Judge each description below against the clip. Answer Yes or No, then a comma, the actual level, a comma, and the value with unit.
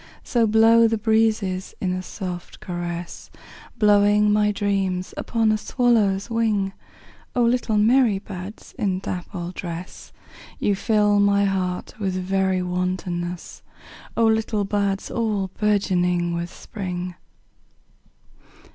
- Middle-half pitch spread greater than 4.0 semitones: No, average, 2.8 semitones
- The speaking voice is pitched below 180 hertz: No, high, 200 Hz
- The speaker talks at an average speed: No, slow, 100 wpm